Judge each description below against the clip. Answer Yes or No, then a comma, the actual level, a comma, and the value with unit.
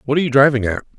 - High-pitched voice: No, low, 135 Hz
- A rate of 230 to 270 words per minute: No, fast, 305 wpm